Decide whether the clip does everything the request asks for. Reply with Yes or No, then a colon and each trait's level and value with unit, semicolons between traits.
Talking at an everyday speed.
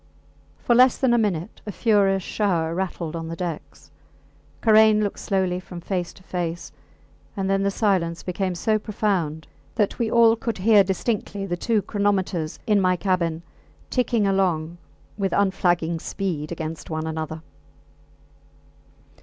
Yes: average, 145 wpm